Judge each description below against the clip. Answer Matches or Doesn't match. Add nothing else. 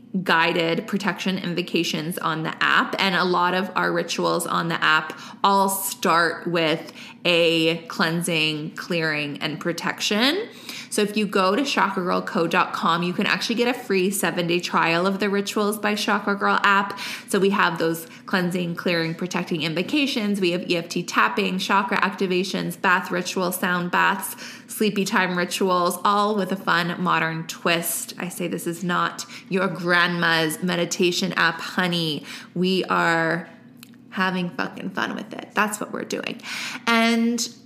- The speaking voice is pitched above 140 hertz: Matches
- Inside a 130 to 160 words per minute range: Matches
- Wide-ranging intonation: Doesn't match